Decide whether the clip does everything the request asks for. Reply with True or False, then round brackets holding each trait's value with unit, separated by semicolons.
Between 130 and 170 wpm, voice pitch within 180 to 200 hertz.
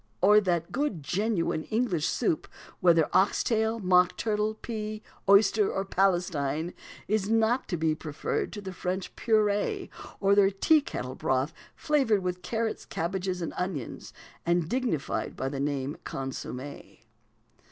True (140 wpm; 190 Hz)